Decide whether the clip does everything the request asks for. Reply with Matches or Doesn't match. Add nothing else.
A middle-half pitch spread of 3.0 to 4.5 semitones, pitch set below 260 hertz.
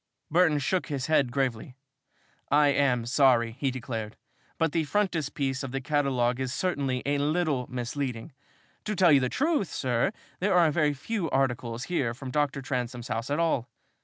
Matches